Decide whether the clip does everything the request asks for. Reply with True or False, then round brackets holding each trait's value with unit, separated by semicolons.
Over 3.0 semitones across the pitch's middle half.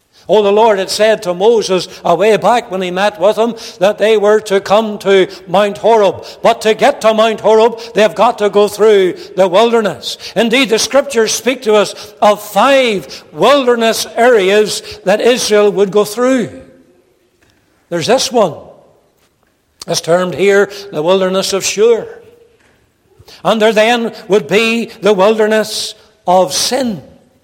False (2.5 semitones)